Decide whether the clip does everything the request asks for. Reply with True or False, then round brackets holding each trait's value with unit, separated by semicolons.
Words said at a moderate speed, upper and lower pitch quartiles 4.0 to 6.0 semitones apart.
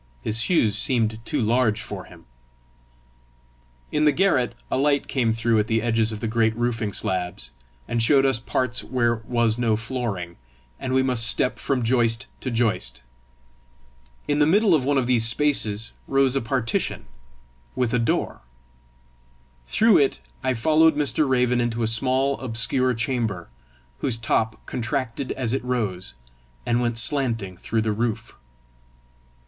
False (155 wpm; 2.8 semitones)